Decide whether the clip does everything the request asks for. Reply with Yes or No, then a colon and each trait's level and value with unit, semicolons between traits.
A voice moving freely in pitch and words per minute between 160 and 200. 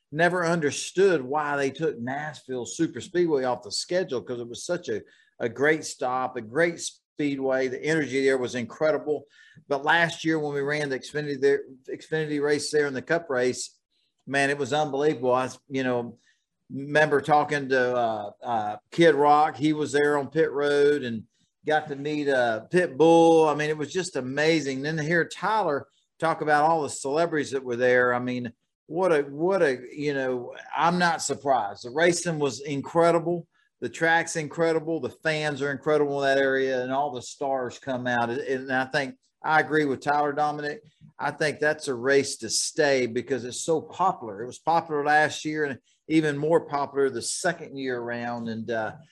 No: average, 3.2 semitones; average, 190 wpm